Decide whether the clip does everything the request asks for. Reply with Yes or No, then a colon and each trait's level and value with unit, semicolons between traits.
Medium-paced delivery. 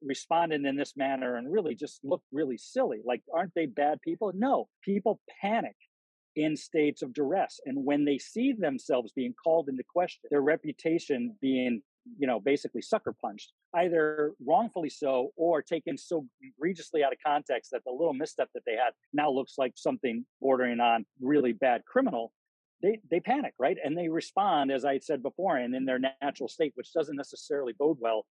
Yes: average, 180 wpm